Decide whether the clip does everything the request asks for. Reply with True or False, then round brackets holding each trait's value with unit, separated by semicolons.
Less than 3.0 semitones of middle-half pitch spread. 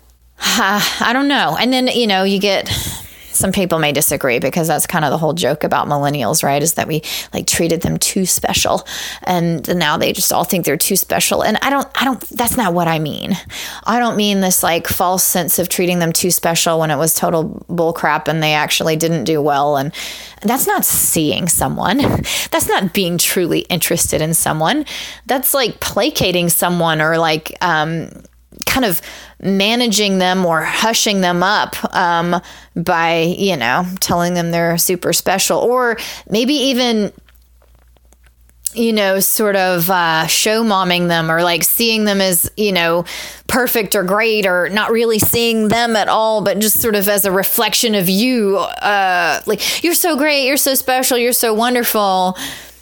False (5.1 semitones)